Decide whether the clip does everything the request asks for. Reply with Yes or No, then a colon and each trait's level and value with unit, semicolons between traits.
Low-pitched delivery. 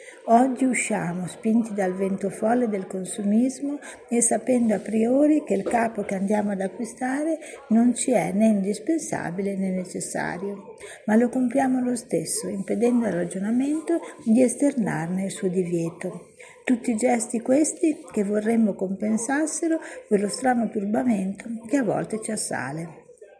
No: high, 225 Hz